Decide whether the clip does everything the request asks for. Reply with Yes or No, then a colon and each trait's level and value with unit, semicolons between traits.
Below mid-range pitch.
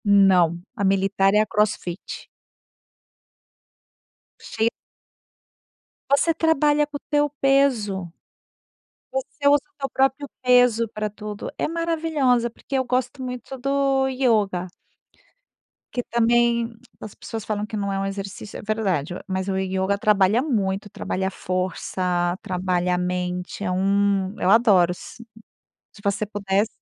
No: high, 210 Hz